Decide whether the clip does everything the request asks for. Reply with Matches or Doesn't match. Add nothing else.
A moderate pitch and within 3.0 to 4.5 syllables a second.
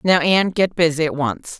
Doesn't match